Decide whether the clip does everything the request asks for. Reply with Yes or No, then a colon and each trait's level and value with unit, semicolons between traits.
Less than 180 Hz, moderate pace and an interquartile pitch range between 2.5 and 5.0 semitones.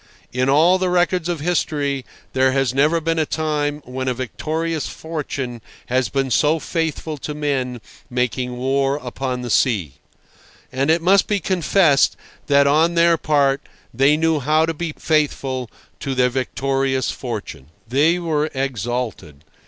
Yes: medium, 140 Hz; average, 150 wpm; average, 3.7 semitones